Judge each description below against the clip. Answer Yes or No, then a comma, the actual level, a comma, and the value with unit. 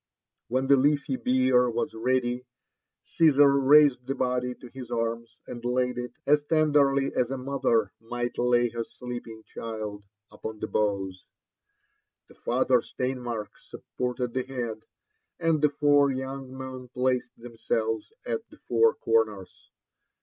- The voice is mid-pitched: No, low, 125 Hz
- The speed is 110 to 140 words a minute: Yes, slow, 135 wpm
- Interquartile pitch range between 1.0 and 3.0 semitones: Yes, narrow, 2.6 semitones